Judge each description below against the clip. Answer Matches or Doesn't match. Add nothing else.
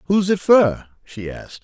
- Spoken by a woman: Doesn't match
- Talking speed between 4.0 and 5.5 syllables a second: Matches